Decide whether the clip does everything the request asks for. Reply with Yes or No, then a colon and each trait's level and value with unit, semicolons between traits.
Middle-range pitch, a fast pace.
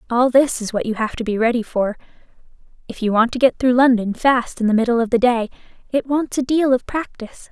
No: high, 240 Hz; fast, 240 wpm